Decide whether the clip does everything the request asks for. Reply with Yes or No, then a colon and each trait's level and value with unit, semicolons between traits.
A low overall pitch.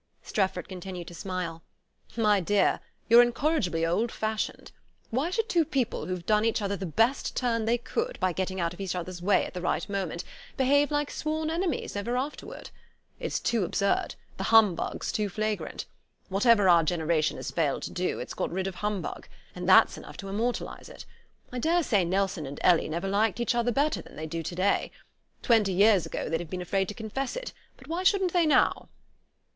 No: high, 205 Hz